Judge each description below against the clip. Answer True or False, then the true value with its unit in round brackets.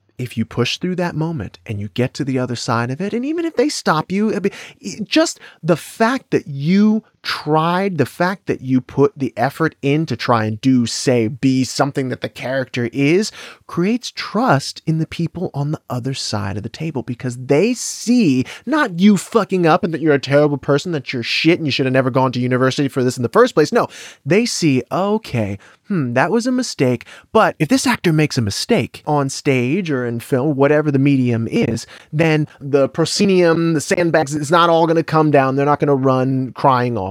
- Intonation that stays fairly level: False (5.3 semitones)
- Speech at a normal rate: False (215 wpm)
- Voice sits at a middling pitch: True (145 Hz)